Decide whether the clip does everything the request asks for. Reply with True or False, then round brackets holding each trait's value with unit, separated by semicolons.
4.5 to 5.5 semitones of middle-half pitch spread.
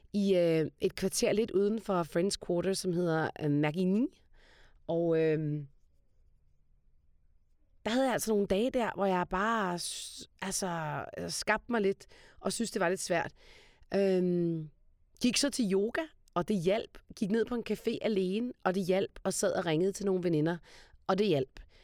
True (4.8 semitones)